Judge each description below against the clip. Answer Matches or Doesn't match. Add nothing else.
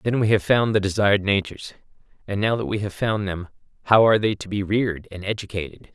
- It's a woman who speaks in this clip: Doesn't match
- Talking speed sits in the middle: Doesn't match